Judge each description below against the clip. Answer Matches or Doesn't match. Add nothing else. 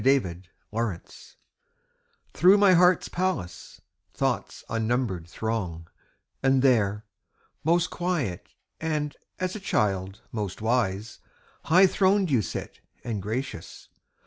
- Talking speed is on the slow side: Matches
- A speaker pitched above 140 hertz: Doesn't match